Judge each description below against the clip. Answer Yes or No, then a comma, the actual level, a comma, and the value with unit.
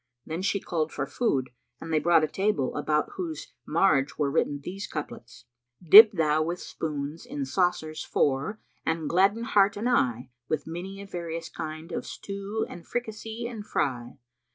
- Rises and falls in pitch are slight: No, average, 5.3 semitones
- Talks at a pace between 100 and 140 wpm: No, average, 170 wpm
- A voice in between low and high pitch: Yes, medium, 165 Hz